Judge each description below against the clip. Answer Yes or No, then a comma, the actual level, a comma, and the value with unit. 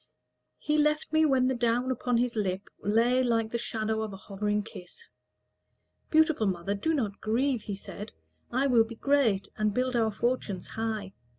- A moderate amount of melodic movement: Yes, average, 3.6 semitones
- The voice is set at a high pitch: Yes, high, 230 Hz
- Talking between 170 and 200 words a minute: Yes, average, 175 wpm